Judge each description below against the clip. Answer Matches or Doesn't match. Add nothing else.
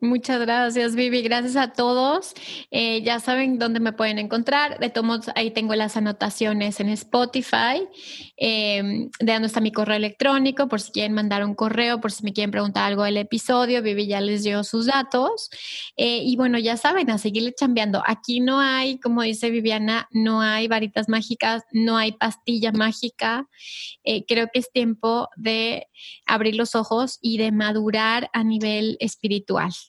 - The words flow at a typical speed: Matches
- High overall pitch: Matches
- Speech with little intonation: Matches